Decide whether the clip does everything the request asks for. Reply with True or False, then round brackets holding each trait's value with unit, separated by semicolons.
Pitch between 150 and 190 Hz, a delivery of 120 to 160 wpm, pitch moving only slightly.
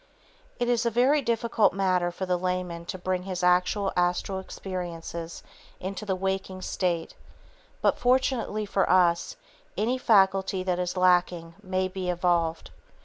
True (185 Hz; 145 wpm; 1.9 semitones)